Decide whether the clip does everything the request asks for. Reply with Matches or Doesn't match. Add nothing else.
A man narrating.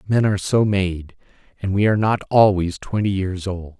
Matches